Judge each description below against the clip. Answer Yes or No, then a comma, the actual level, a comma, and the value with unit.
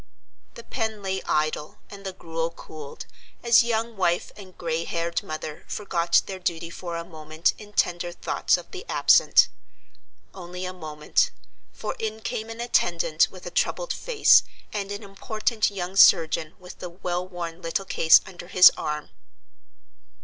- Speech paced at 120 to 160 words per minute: Yes, average, 155 wpm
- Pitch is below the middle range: No, medium, 180 Hz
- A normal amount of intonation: Yes, average, 3.7 semitones